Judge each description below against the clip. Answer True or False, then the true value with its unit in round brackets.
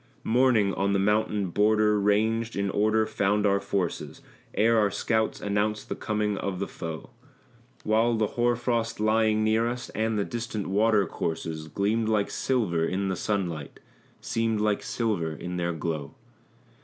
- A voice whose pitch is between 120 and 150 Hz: False (105 Hz)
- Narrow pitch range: True (2.1 semitones)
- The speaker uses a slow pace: False (155 wpm)